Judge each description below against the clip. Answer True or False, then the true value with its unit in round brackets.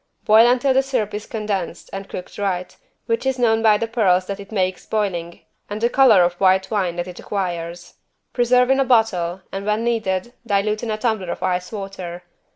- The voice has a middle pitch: False (205 Hz)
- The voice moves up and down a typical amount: True (3.7 semitones)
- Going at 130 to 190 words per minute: False (200 wpm)